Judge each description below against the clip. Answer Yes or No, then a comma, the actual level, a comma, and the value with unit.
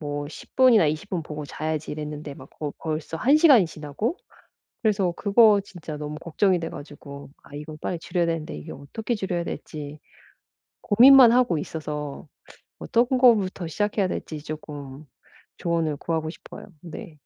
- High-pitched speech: No, medium, 160 Hz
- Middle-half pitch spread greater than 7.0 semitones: No, average, 5.2 semitones